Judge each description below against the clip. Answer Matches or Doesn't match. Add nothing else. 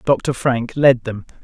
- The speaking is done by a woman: Doesn't match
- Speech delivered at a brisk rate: Doesn't match